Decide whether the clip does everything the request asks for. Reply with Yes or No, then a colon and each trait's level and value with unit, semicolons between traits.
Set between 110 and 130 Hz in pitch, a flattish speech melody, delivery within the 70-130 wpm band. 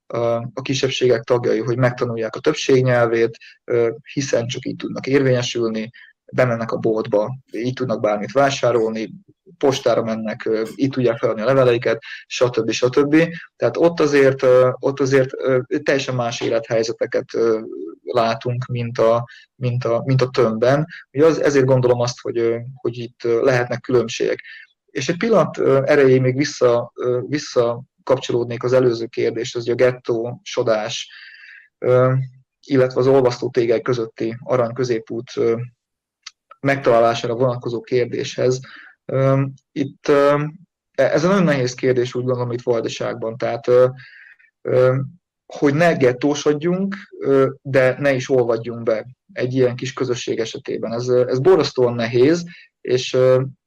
Yes: low, 125 Hz; narrow, 2.3 semitones; average, 120 wpm